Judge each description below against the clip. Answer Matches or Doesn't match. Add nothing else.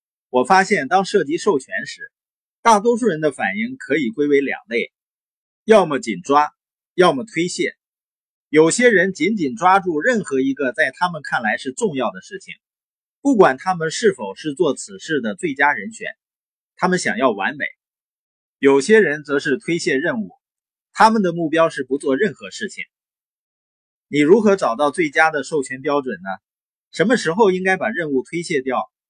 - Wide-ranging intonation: Matches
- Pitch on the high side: Doesn't match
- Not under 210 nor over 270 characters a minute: Matches